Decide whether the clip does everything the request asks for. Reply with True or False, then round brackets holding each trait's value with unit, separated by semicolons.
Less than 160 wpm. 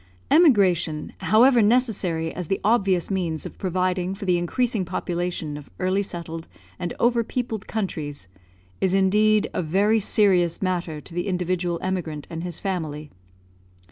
True (140 wpm)